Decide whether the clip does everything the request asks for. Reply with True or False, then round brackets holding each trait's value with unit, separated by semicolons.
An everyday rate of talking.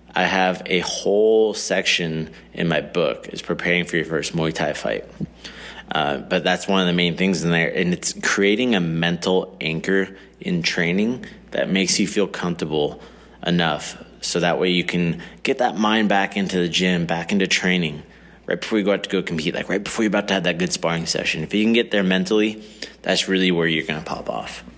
False (215 wpm)